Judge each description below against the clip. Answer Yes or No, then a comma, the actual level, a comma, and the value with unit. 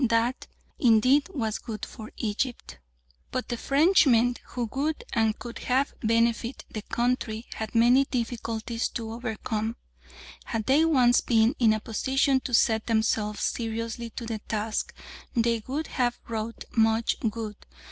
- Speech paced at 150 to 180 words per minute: No, average, 140 wpm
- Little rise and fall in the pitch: Yes, narrow, 2.2 semitones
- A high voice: Yes, high, 230 Hz